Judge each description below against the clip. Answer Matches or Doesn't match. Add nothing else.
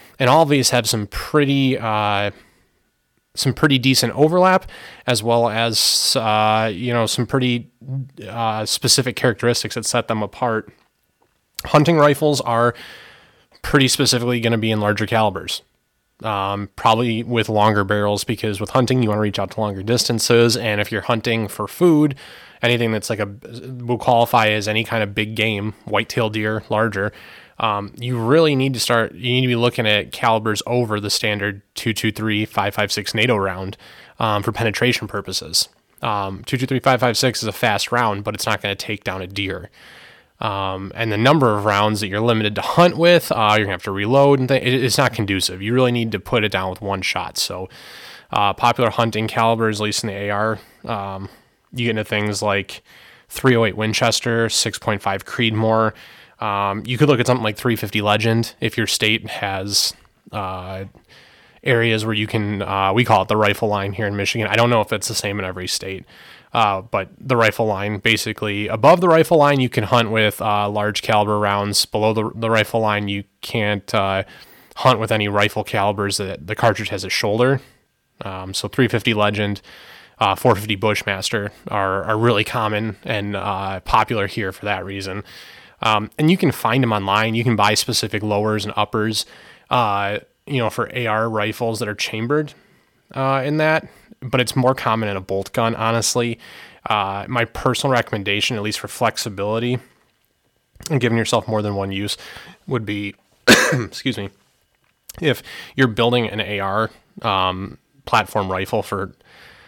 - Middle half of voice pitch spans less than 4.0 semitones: Matches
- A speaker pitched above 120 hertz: Doesn't match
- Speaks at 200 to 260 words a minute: Doesn't match